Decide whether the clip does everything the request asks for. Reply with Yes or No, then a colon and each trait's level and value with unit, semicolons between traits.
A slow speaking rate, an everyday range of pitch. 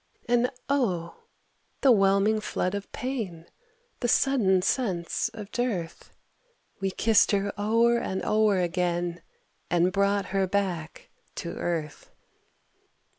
Yes: slow, 115 wpm; average, 4.0 semitones